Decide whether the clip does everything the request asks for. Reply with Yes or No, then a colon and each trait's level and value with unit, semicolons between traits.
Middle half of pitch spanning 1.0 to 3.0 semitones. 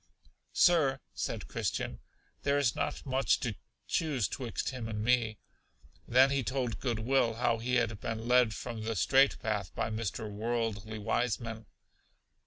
Yes: average, 2.7 semitones